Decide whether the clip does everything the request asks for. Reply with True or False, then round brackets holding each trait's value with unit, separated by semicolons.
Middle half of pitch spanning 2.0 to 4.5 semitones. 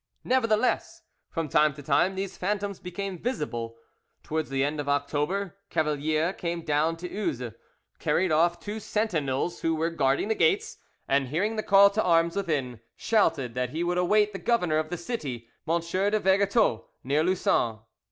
False (5.3 semitones)